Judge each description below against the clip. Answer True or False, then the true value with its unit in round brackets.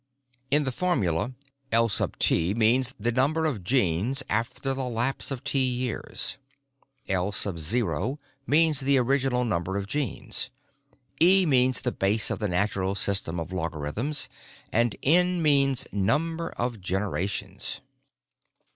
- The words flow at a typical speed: False (120 wpm)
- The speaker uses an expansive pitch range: True (5.9 semitones)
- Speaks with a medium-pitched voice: False (120 Hz)